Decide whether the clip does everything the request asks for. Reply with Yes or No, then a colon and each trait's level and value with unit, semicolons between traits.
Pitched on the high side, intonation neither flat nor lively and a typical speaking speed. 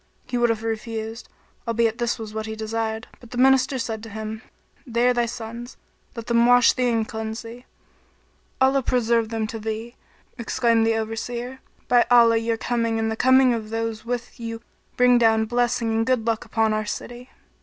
No: high, 230 Hz; narrow, 1.5 semitones; average, 185 wpm